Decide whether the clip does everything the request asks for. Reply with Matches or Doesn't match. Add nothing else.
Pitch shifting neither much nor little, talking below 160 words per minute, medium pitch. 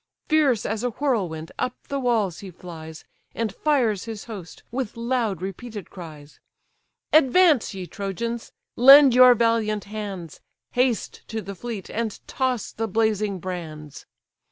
Doesn't match